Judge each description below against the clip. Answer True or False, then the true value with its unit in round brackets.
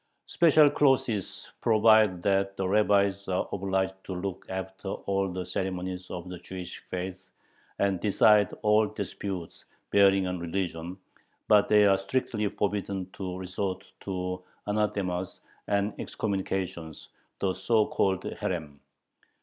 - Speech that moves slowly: True (125 wpm)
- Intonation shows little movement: True (1.8 semitones)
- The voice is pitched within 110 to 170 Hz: False (95 Hz)